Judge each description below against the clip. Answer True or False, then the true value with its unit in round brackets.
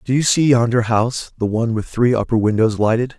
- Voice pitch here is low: True (115 Hz)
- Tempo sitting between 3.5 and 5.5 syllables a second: False (6.1 syllables/s)